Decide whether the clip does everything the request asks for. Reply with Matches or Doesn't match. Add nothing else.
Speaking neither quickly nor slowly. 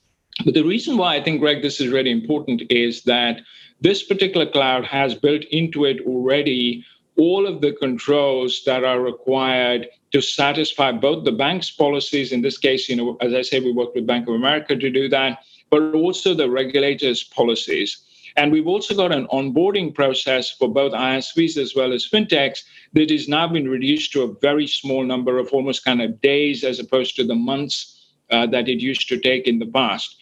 Matches